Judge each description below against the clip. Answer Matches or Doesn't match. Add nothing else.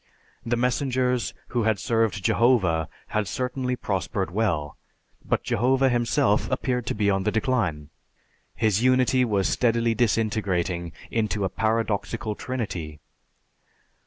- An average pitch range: Matches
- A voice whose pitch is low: Matches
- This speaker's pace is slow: Matches